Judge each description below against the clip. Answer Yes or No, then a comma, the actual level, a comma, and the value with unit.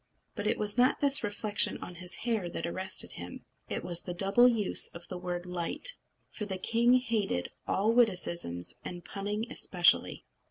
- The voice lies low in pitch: No, high, 195 Hz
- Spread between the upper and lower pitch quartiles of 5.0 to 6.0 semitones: No, average, 4.3 semitones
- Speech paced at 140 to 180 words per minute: Yes, average, 170 wpm